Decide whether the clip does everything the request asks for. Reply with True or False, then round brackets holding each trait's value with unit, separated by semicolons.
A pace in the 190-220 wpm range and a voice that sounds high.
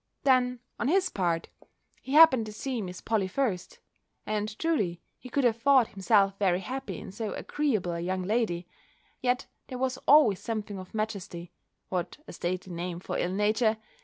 False (170 wpm; 215 Hz)